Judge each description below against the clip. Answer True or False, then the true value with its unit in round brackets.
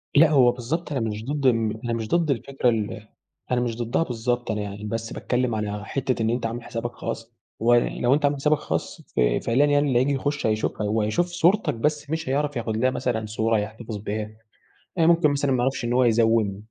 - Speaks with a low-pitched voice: True (120 Hz)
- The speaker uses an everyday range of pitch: True (4.2 semitones)